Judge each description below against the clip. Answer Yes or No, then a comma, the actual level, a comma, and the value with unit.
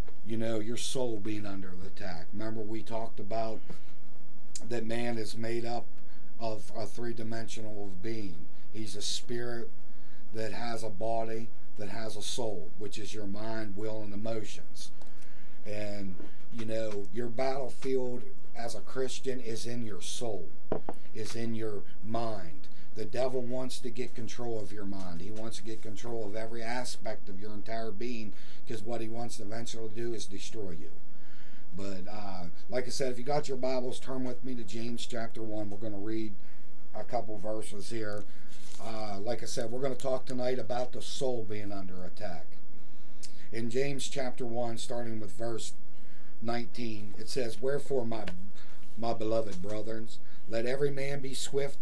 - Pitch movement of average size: No, narrow, 2.3 semitones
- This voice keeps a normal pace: Yes, average, 170 wpm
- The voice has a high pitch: No, low, 115 Hz